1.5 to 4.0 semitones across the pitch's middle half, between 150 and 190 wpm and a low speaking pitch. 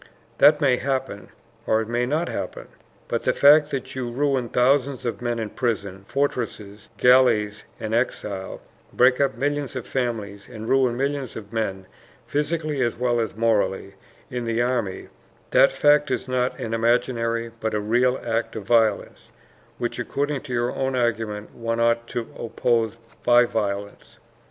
Yes: average, 2.8 semitones; average, 160 wpm; low, 120 Hz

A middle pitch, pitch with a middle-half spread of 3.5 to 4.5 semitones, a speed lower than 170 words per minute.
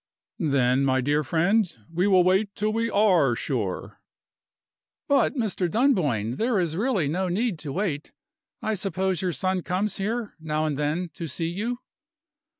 No: medium, 180 Hz; wide, 5.6 semitones; average, 155 wpm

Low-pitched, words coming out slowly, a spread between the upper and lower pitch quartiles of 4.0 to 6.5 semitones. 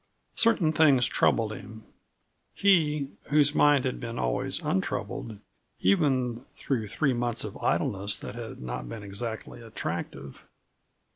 Yes: low, 120 Hz; slow, 125 wpm; average, 5.1 semitones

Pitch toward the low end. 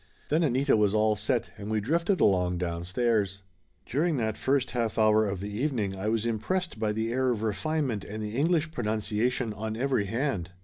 Yes: low, 110 Hz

